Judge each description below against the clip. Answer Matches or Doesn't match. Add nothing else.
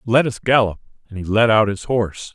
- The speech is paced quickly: Matches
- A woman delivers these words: Doesn't match